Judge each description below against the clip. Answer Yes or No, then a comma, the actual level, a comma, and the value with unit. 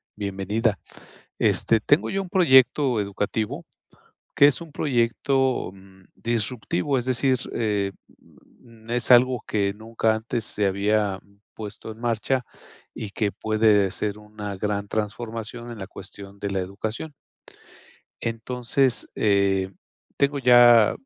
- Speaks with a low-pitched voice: Yes, low, 110 Hz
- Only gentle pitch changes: No, average, 3.3 semitones